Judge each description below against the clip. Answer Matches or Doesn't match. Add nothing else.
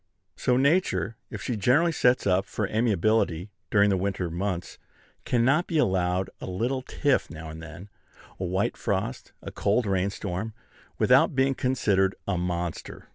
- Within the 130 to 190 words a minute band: Matches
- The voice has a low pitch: Matches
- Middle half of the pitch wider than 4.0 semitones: Matches